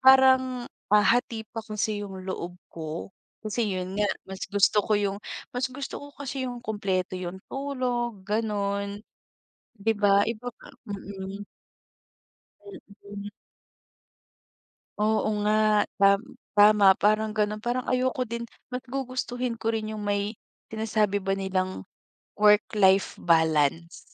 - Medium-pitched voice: No, high, 210 Hz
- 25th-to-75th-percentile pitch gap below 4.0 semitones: Yes, average, 3.3 semitones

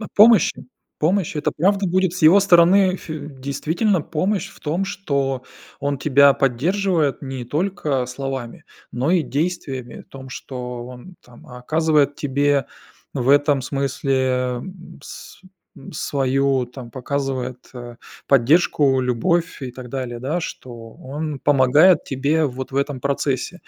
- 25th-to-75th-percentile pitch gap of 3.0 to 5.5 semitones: Yes, average, 4.2 semitones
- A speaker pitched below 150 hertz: Yes, medium, 140 Hz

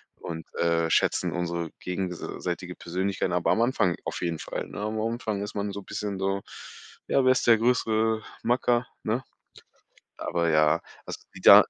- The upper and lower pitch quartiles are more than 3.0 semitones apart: Yes, average, 4.5 semitones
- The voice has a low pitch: Yes, low, 100 Hz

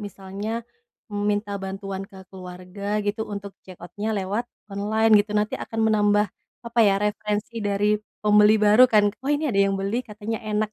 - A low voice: No, high, 210 Hz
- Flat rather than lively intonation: Yes, narrow, 1.5 semitones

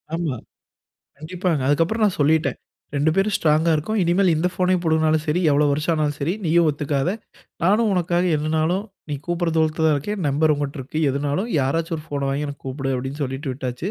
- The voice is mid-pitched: Yes, medium, 155 Hz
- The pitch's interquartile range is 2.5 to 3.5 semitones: Yes, average, 3.2 semitones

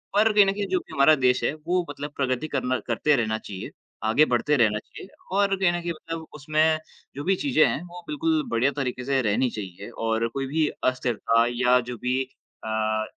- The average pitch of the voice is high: No, medium, 140 Hz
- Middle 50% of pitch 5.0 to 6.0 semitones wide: Yes, wide, 5.6 semitones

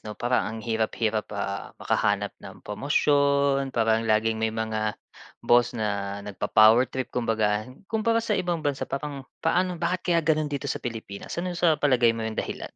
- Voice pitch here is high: No, low, 120 Hz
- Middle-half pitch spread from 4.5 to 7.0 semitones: Yes, average, 5.2 semitones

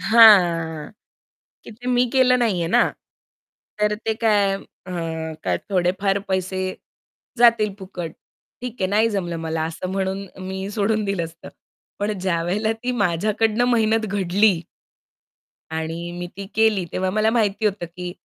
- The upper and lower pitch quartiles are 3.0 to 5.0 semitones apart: Yes, average, 3.7 semitones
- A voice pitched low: No, high, 200 Hz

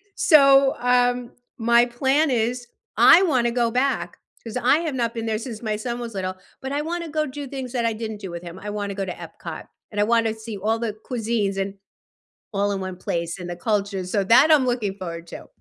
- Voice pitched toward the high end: Yes, high, 230 Hz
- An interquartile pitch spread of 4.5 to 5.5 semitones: No, average, 4.0 semitones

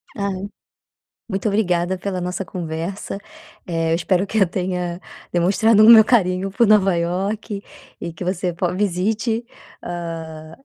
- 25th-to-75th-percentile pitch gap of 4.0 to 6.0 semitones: No, average, 2.7 semitones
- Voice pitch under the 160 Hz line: No, medium, 185 Hz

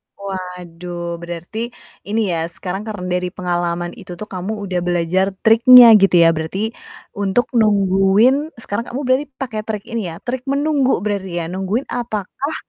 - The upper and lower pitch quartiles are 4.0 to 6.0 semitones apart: Yes, average, 4.6 semitones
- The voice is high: Yes, high, 195 Hz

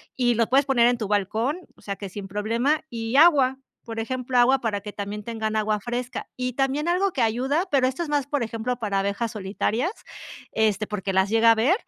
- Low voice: No, high, 235 Hz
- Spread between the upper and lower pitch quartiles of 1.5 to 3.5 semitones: No, average, 3.9 semitones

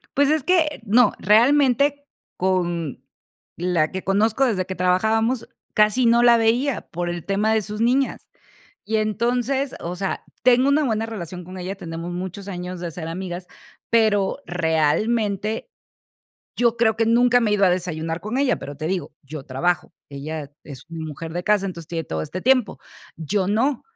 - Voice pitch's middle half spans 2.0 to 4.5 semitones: No, average, 5.2 semitones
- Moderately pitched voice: No, high, 200 Hz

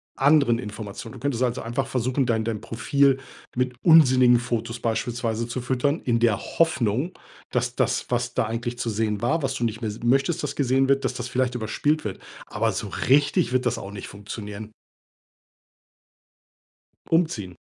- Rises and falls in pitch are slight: No, average, 3.2 semitones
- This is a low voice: Yes, low, 120 Hz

